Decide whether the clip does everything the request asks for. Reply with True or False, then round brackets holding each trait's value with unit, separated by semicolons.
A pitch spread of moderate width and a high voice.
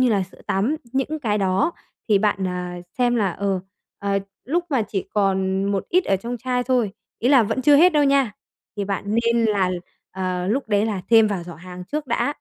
True (4.9 semitones; 210 Hz)